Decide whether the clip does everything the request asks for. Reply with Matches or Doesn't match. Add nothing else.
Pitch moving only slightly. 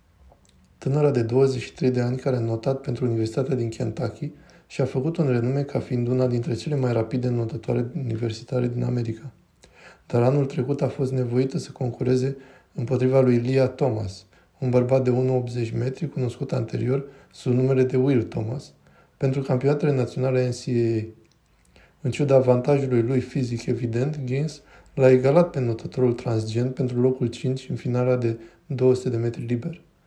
Matches